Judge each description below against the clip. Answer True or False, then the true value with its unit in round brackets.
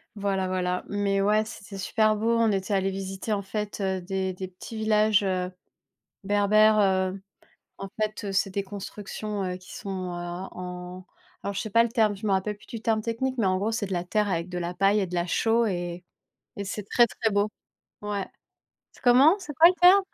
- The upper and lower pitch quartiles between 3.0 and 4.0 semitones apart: False (2.4 semitones)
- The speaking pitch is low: False (200 Hz)